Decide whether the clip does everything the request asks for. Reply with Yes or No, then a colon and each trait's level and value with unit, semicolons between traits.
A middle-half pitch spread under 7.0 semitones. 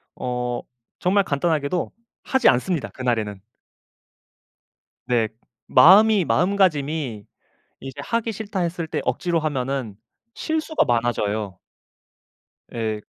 No: wide, 7.4 semitones